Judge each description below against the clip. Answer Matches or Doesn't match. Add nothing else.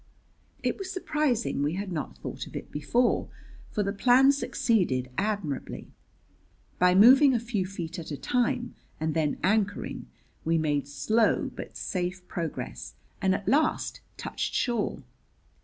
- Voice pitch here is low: Doesn't match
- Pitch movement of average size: Doesn't match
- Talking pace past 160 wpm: Doesn't match